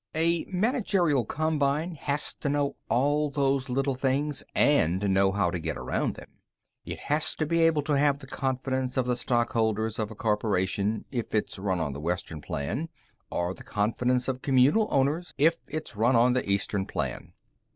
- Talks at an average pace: Yes, average, 180 wpm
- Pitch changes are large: Yes, wide, 5.9 semitones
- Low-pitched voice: Yes, low, 130 Hz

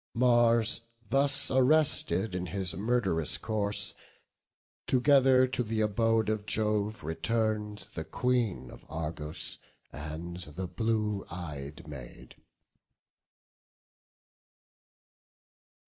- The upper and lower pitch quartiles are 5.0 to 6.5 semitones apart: Yes, wide, 5.6 semitones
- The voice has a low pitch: Yes, low, 105 Hz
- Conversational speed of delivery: No, slow, 85 wpm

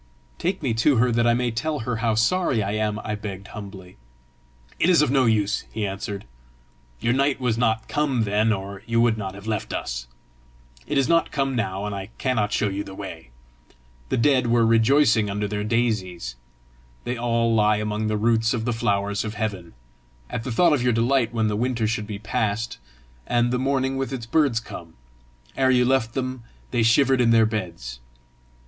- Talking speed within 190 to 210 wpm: Yes, average, 195 wpm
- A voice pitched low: Yes, low, 115 Hz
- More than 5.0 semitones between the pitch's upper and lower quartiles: No, average, 3.2 semitones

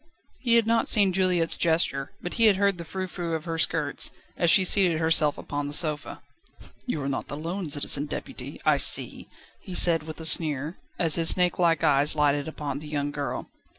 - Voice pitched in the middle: Yes, medium, 160 Hz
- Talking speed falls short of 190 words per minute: No, average, 195 wpm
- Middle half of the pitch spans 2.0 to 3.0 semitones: No, average, 3.4 semitones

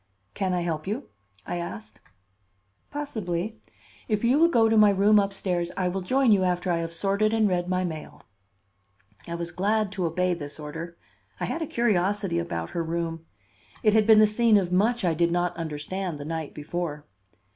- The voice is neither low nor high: Yes, medium, 180 Hz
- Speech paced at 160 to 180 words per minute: No, average, 190 wpm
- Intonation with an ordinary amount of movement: Yes, average, 4.0 semitones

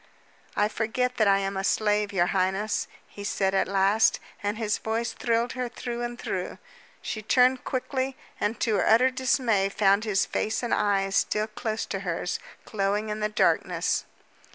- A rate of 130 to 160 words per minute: No, average, 175 wpm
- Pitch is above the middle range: Yes, high, 215 Hz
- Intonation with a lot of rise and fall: No, average, 3.1 semitones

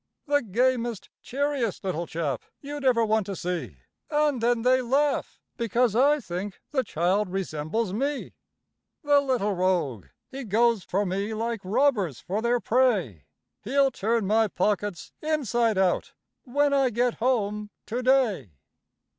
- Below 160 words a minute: Yes, average, 140 wpm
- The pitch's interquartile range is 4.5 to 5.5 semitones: Yes, average, 5.1 semitones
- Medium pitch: No, high, 230 Hz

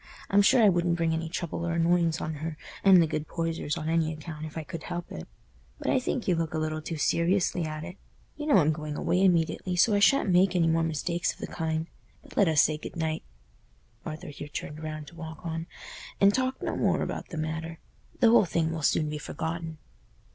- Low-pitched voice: No, medium, 165 Hz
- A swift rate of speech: Yes, fast, 220 wpm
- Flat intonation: Yes, narrow, 2.0 semitones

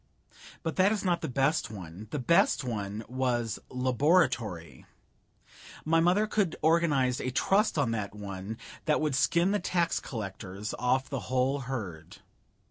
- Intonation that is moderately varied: No, wide, 7.2 semitones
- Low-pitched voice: Yes, low, 130 Hz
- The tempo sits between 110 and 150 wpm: Yes, average, 145 wpm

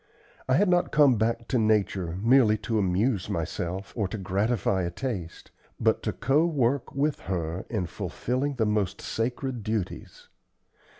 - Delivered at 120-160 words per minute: Yes, average, 155 wpm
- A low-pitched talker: Yes, low, 110 Hz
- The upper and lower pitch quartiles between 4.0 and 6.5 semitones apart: Yes, average, 5.3 semitones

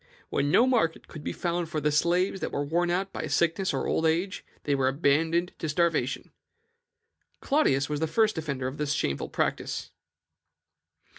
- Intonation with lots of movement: No, average, 3.4 semitones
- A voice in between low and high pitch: Yes, medium, 160 Hz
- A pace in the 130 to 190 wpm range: Yes, average, 170 wpm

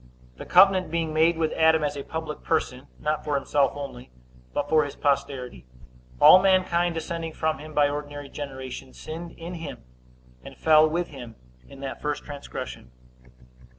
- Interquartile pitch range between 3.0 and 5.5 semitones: No, narrow, 2.5 semitones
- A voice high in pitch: No, medium, 155 Hz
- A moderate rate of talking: Yes, average, 160 wpm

